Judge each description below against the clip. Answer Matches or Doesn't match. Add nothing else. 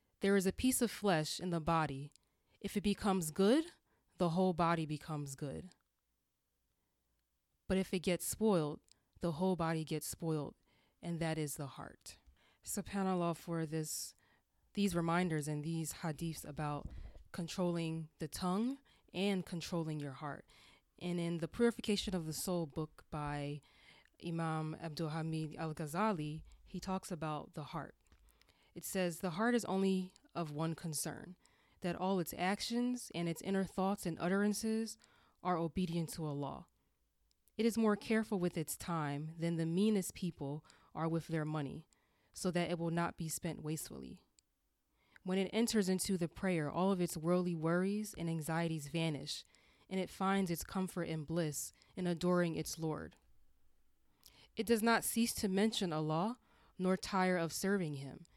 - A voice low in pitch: Doesn't match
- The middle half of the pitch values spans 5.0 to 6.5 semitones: Doesn't match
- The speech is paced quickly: Doesn't match